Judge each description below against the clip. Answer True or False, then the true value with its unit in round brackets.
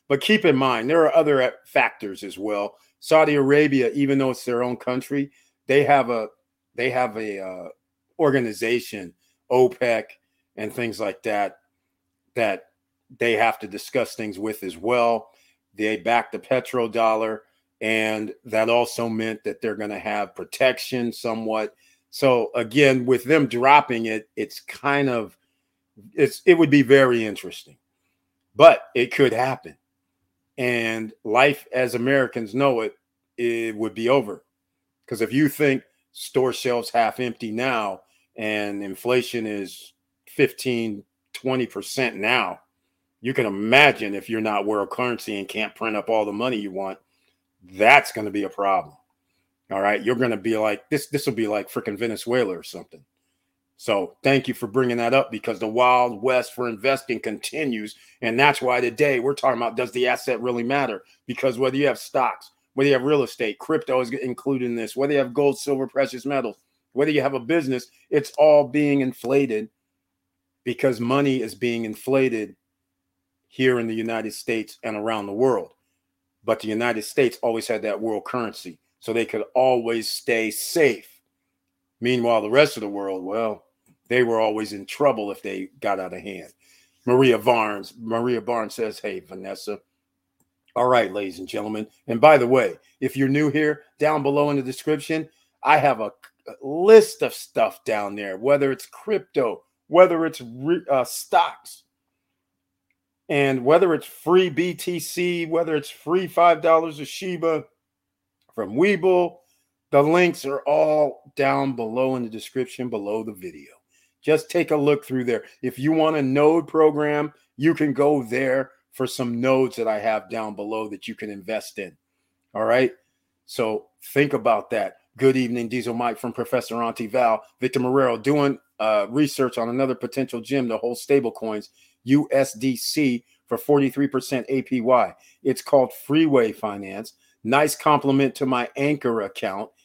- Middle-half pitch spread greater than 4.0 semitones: True (4.5 semitones)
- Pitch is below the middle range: True (125 Hz)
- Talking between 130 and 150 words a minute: False (160 wpm)